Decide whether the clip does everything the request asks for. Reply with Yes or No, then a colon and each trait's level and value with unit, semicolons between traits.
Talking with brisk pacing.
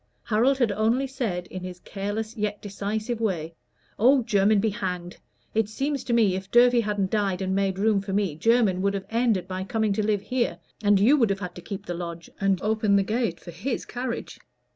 Yes: fast, 210 wpm